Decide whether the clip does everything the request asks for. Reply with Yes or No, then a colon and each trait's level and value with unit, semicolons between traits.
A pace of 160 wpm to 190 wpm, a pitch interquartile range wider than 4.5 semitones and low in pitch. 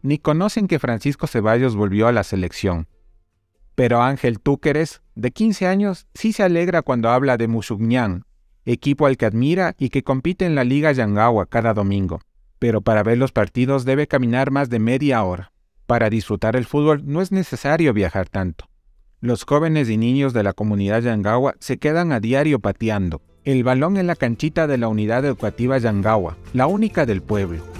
Yes: average, 175 wpm; wide, 5.5 semitones; low, 120 Hz